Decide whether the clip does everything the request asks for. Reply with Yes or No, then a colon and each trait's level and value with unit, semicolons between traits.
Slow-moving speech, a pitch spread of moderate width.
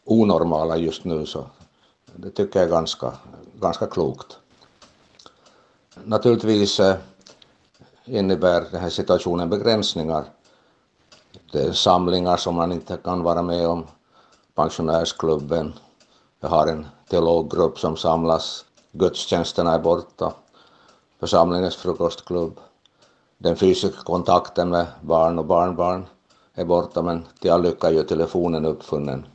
No: slow, 110 wpm; narrow, 2.0 semitones